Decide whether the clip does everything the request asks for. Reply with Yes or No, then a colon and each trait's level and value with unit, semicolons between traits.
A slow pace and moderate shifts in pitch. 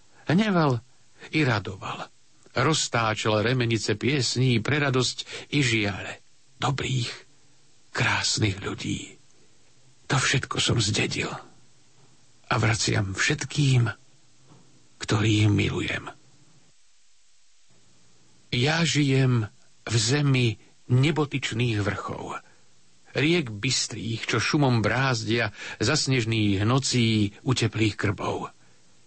Yes: slow, 80 wpm; average, 3.8 semitones